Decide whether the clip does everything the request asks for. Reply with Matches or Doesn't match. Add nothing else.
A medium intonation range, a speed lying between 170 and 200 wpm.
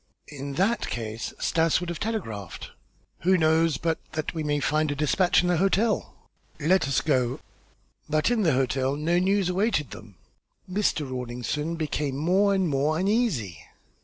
Doesn't match